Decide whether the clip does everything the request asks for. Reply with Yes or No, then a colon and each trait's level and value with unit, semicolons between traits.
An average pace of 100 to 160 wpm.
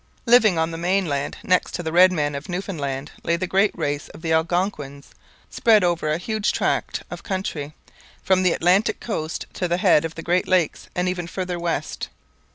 No: average, 190 wpm